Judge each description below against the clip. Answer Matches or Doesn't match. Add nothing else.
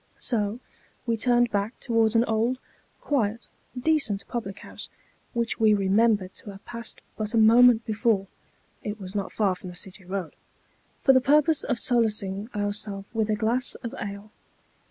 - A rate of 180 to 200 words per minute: Doesn't match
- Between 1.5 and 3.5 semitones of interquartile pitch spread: Matches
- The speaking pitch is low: Doesn't match